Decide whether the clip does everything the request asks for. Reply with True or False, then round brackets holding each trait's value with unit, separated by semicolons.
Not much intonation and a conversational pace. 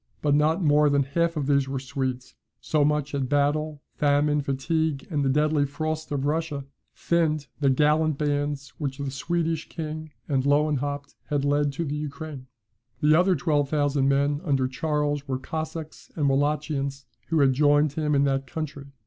True (1.7 semitones; 170 wpm)